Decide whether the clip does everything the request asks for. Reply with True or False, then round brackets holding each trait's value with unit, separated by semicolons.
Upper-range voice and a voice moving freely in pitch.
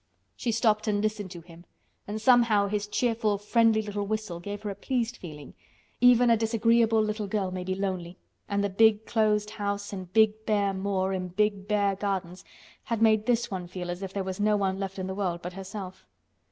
False (205 Hz; 2.4 semitones)